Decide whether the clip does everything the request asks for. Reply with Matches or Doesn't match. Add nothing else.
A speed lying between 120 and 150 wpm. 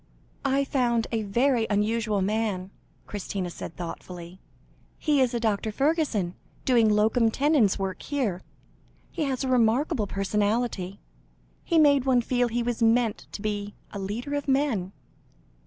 Matches